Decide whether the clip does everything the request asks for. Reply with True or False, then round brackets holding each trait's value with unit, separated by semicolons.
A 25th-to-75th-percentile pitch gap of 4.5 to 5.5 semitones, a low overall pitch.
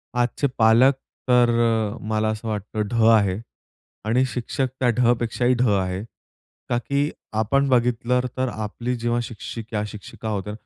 False (2.5 semitones; 115 Hz)